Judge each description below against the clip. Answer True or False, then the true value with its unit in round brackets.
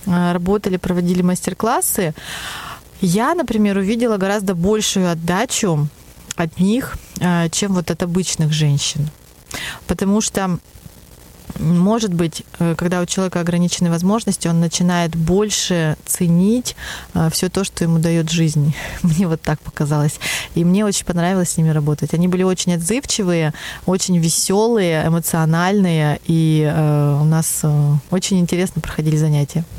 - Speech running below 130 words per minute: True (120 wpm)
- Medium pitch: True (175 Hz)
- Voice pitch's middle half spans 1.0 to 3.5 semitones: True (3.0 semitones)